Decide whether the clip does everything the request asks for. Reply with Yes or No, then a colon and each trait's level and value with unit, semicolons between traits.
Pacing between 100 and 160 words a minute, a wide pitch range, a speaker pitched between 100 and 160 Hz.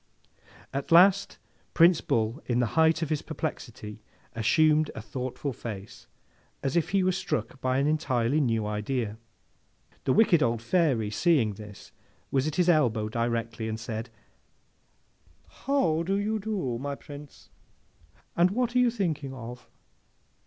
Yes: average, 145 wpm; wide, 6.6 semitones; medium, 140 Hz